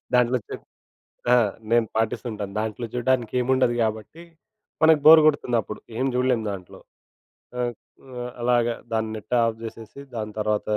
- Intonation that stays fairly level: Yes, narrow, 2.2 semitones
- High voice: No, low, 120 Hz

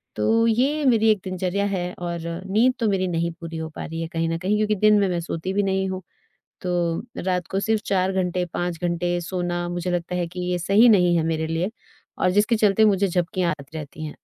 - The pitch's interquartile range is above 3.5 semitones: No, average, 2.8 semitones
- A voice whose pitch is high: No, medium, 180 Hz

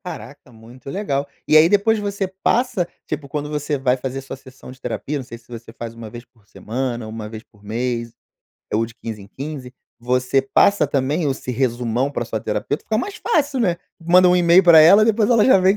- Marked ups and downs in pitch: Yes, wide, 7.1 semitones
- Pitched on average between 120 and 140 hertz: Yes, low, 135 Hz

